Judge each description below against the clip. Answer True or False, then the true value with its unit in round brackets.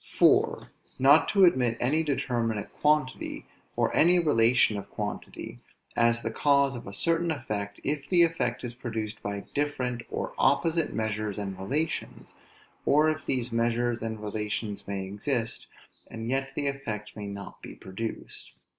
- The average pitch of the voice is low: True (120 Hz)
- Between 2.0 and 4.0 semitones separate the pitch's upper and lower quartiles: False (5.1 semitones)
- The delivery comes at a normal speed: True (150 wpm)